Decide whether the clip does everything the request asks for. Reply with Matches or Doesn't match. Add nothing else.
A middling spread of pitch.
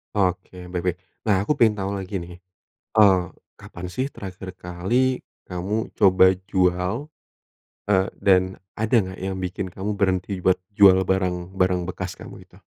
Doesn't match